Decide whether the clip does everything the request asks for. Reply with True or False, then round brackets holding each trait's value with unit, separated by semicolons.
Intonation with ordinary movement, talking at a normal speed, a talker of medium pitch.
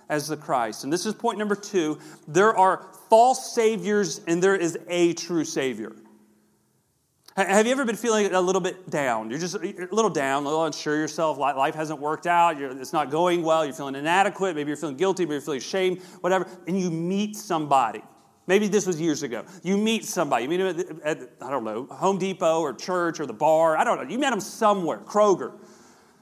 False (4.2 semitones; 210 wpm; 175 Hz)